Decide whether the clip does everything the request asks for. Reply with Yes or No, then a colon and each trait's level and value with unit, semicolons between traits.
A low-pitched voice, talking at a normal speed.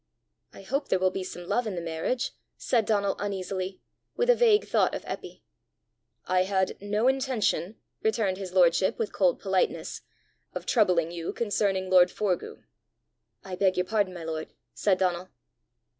No: high, 190 Hz; average, 160 wpm